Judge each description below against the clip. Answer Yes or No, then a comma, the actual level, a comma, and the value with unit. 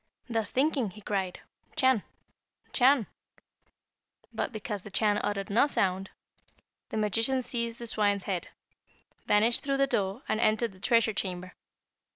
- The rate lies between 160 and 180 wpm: No, average, 140 wpm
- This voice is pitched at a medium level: No, high, 215 Hz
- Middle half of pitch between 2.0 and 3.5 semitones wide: Yes, average, 3.2 semitones